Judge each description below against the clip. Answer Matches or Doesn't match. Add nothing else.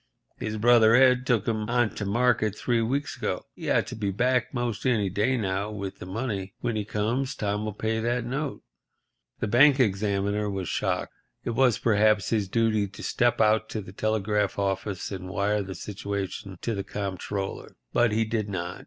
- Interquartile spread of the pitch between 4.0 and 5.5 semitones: Doesn't match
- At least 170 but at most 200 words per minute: Matches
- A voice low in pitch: Matches